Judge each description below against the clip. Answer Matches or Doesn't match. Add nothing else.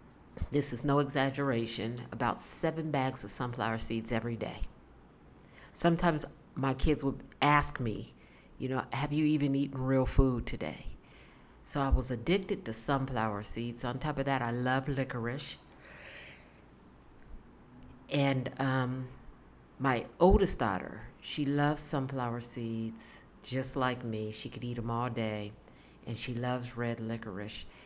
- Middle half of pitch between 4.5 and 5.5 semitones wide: Doesn't match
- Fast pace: Doesn't match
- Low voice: Matches